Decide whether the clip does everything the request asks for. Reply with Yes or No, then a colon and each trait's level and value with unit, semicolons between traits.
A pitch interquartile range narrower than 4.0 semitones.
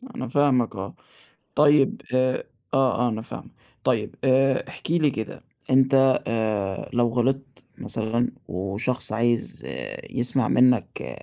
Yes: average, 3.2 semitones